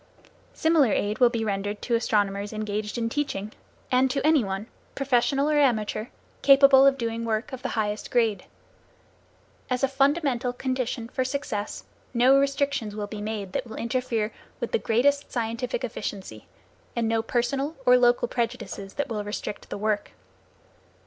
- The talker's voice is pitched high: Yes, high, 235 Hz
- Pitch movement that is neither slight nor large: Yes, average, 4.2 semitones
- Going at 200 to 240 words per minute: No, average, 155 wpm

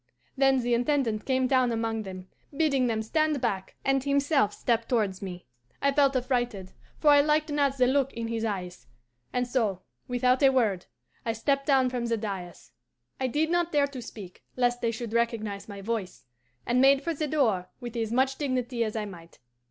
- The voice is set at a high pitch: Yes, high, 245 Hz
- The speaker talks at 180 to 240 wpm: Yes, average, 190 wpm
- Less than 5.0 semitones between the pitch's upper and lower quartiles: Yes, average, 3.9 semitones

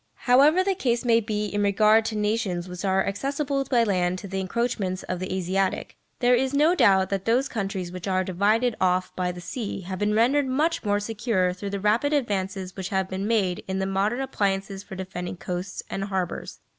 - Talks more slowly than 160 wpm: No, fast, 205 wpm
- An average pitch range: Yes, average, 3.9 semitones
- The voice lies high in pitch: Yes, high, 200 Hz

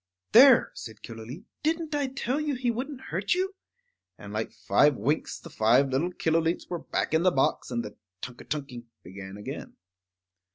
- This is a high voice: No, medium, 160 Hz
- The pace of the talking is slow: No, average, 175 wpm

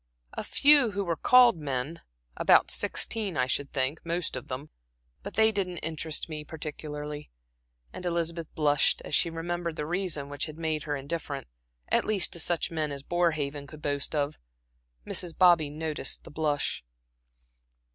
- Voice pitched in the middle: Yes, medium, 155 Hz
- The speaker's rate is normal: Yes, average, 160 wpm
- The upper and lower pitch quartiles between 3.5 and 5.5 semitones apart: No, average, 2.9 semitones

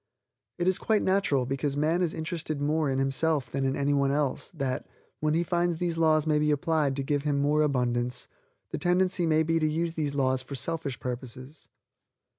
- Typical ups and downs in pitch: Yes, average, 3.1 semitones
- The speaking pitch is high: No, medium, 150 Hz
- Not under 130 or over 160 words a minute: No, average, 200 wpm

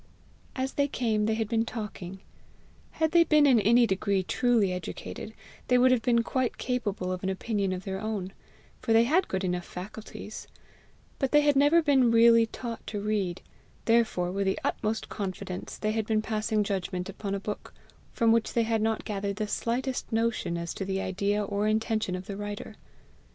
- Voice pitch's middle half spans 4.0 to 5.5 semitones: No, average, 3.2 semitones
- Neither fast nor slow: Yes, average, 190 wpm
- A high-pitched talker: Yes, high, 215 Hz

